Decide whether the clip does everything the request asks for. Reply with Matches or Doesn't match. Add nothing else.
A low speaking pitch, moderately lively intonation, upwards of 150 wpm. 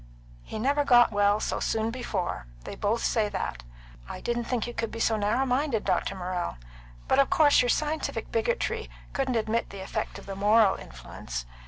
Doesn't match